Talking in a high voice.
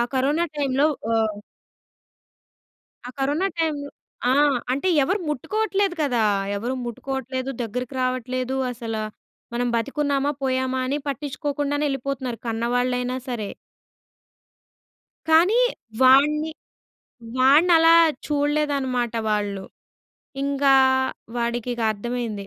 Yes: very high, 260 Hz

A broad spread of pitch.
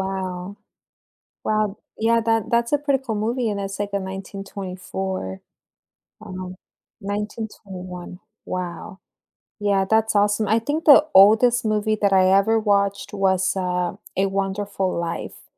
No: narrow, 2.5 semitones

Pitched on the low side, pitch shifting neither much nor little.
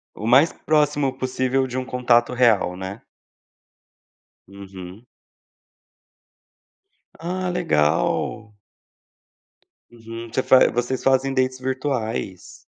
Yes: low, 125 Hz; average, 3.3 semitones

